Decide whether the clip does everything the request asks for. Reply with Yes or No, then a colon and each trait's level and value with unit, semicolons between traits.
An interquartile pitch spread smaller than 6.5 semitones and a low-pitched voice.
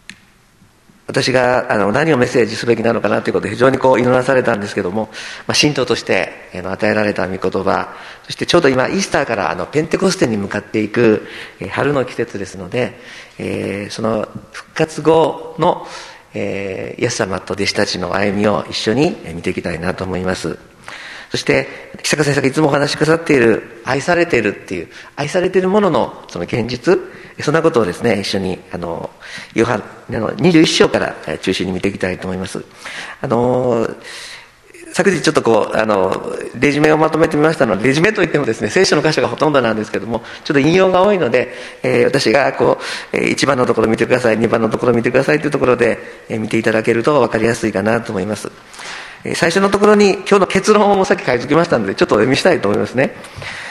No: wide, 7.1 semitones; low, 115 Hz